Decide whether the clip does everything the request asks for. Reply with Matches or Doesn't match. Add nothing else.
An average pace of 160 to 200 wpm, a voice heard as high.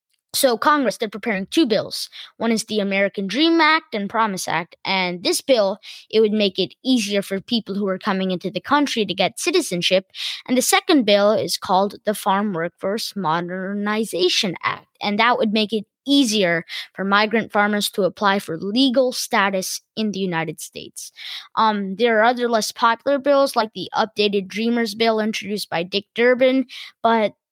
Matches